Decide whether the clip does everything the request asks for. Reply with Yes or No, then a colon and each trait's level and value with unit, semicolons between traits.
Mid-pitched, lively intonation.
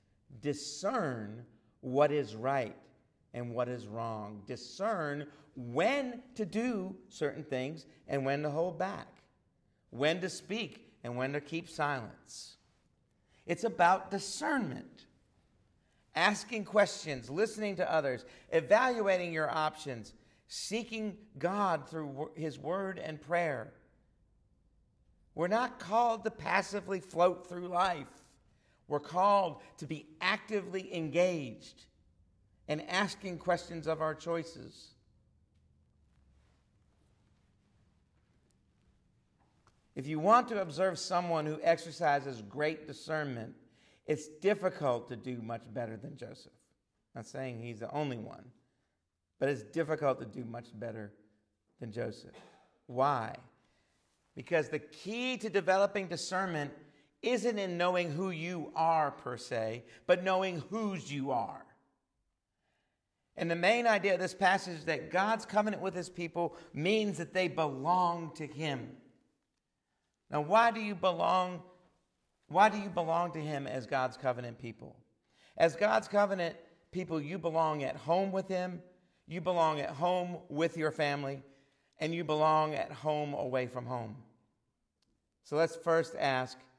Yes: medium, 155 Hz; wide, 6.1 semitones